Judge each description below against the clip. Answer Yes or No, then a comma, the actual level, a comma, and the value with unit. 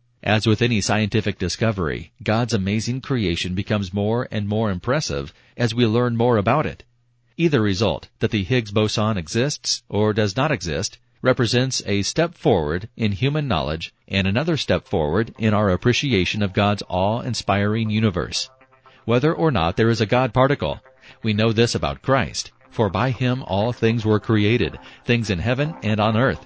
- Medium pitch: No, low, 110 Hz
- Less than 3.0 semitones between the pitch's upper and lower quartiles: No, average, 3.3 semitones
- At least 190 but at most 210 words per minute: No, average, 170 wpm